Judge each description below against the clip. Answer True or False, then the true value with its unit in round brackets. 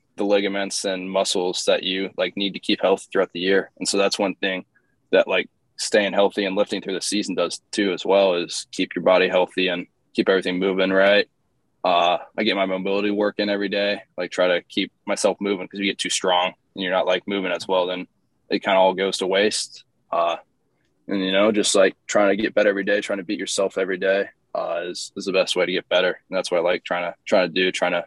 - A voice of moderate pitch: False (95 Hz)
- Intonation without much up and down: True (1.4 semitones)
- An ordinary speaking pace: False (250 wpm)